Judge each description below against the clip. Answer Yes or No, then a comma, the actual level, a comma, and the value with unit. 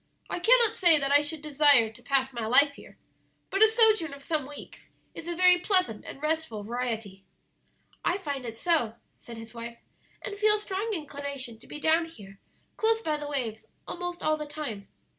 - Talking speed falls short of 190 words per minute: No, average, 195 wpm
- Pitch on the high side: Yes, very high, 295 Hz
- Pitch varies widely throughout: Yes, wide, 6.7 semitones